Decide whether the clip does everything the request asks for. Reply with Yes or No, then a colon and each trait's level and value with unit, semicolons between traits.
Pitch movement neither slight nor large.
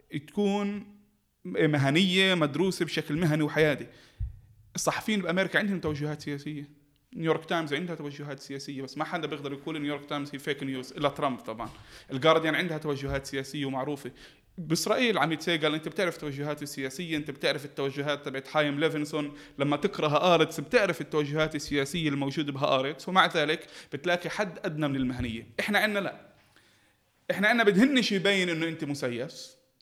Yes: average, 3.2 semitones